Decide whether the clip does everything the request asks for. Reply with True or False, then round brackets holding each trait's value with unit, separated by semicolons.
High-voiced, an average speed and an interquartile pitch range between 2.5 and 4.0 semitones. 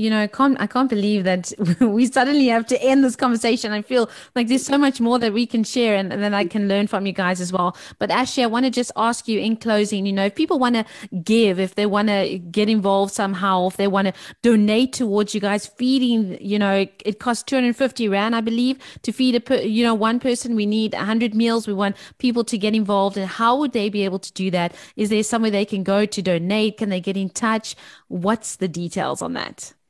False (215 Hz; 245 wpm; 3.3 semitones)